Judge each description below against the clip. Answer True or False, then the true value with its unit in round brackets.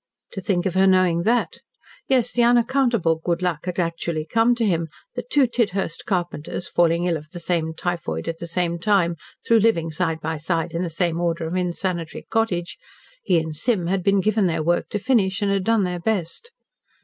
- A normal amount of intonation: True (3.7 semitones)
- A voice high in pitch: False (180 Hz)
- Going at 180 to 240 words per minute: True (200 wpm)